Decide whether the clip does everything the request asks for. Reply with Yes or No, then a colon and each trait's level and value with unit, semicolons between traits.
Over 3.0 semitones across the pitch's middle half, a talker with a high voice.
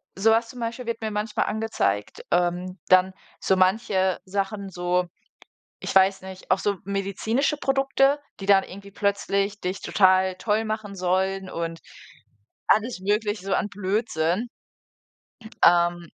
No: average, 2.7 semitones; high, 195 Hz